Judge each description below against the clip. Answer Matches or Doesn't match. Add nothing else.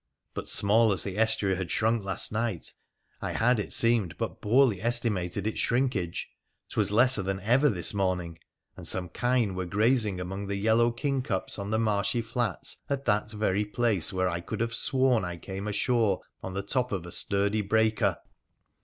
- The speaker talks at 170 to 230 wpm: Matches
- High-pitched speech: Doesn't match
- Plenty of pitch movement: Doesn't match